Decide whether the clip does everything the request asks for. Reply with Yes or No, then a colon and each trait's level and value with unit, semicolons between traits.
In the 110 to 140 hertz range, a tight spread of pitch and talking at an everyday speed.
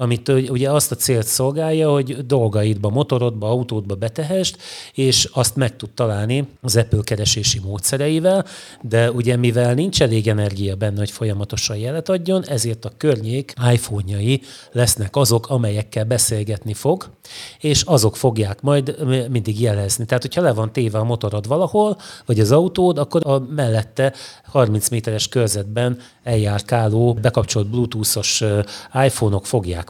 No: low, 120 Hz; average, 4.0 semitones; average, 135 wpm